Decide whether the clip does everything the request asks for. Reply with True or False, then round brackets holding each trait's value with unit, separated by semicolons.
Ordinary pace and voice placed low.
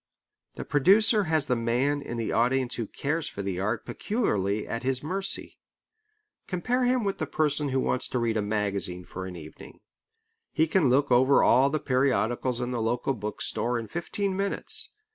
True (180 wpm; 130 Hz)